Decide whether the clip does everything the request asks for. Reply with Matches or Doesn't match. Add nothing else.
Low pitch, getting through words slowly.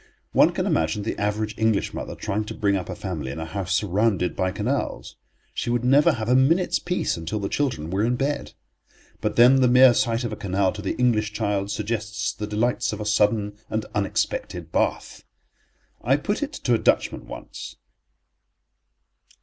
Doesn't match